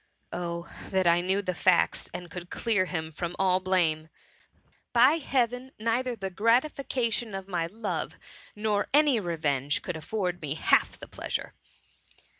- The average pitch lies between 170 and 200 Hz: Yes, high, 190 Hz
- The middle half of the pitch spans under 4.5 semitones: No, average, 4.9 semitones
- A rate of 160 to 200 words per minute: No, average, 150 wpm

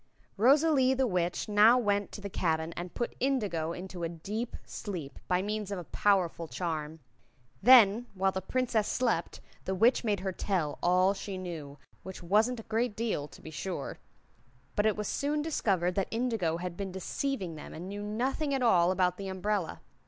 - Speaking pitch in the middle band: No, high, 195 Hz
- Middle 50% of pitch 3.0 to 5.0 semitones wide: Yes, average, 4.4 semitones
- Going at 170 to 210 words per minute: Yes, average, 180 wpm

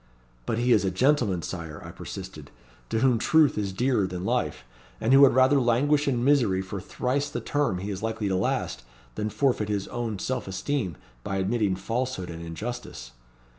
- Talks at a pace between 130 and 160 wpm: No, average, 185 wpm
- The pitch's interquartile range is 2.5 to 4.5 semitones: No, wide, 5.4 semitones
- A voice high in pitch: No, low, 110 Hz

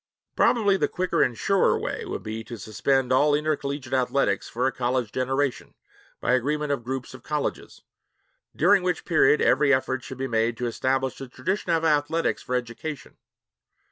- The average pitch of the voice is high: No, low, 135 Hz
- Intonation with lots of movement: No, average, 3.3 semitones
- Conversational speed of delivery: Yes, average, 170 wpm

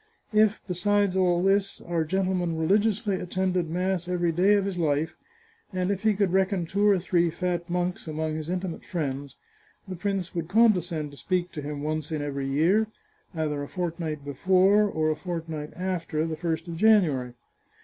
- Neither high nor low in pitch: Yes, medium, 175 Hz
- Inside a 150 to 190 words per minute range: Yes, average, 175 wpm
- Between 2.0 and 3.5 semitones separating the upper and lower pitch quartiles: Yes, average, 3.2 semitones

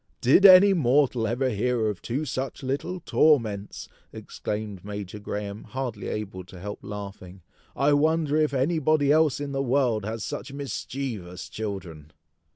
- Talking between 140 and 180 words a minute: Yes, average, 145 wpm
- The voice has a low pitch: Yes, low, 125 Hz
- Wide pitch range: Yes, wide, 5.7 semitones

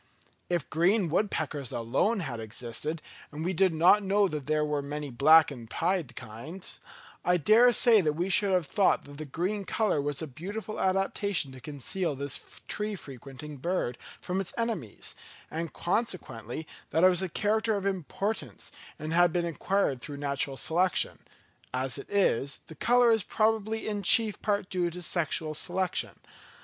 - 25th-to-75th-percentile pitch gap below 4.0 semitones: No, wide, 5.5 semitones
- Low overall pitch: No, medium, 170 Hz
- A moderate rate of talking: Yes, average, 165 wpm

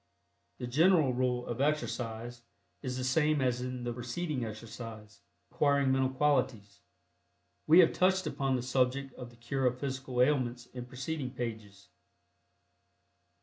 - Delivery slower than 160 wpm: Yes, average, 140 wpm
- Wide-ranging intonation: No, narrow, 2.4 semitones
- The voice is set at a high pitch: No, low, 125 Hz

